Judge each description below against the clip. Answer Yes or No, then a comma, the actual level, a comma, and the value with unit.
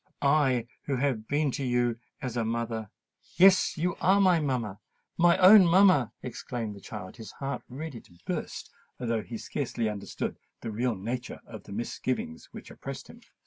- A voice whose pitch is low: Yes, low, 125 Hz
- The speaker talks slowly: No, average, 160 wpm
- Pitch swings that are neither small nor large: Yes, average, 4.8 semitones